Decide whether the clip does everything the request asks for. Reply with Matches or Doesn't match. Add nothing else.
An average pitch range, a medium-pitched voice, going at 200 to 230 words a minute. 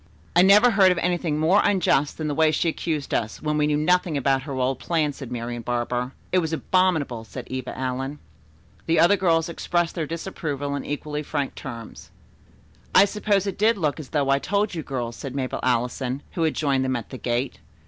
Matches